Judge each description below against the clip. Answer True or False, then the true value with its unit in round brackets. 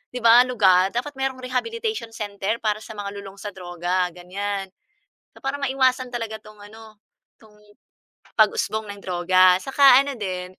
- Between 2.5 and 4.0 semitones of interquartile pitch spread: False (4.7 semitones)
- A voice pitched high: True (215 Hz)